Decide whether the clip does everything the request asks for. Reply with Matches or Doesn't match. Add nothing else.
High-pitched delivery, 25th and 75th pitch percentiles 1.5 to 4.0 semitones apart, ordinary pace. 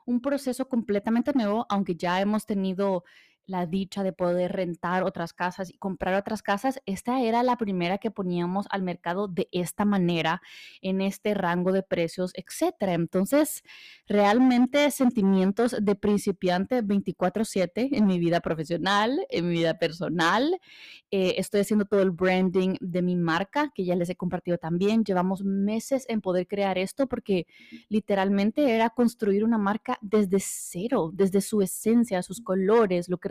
Matches